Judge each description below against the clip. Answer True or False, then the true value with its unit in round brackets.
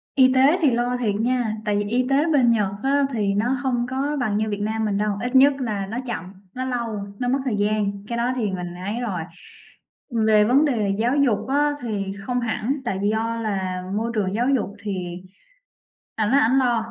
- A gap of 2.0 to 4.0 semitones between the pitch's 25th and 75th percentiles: True (3.7 semitones)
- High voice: True (225 Hz)